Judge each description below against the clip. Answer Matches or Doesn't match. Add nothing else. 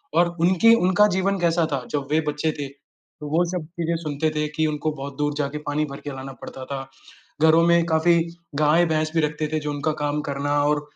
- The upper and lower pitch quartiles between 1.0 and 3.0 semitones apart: Matches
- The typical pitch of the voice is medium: Matches